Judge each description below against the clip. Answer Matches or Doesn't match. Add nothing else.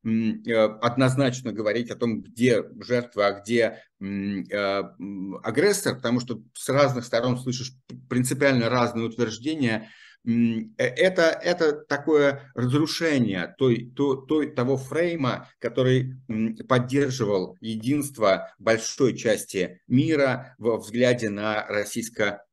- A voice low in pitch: Matches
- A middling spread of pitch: Matches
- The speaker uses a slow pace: Matches